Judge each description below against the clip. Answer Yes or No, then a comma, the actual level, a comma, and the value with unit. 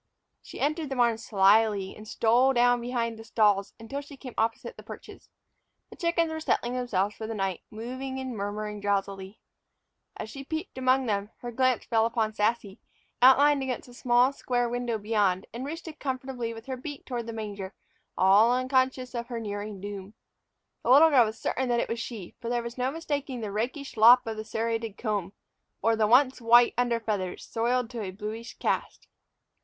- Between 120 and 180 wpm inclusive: No, average, 190 wpm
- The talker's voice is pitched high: Yes, high, 235 Hz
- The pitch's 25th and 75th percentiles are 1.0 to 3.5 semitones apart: Yes, average, 3.2 semitones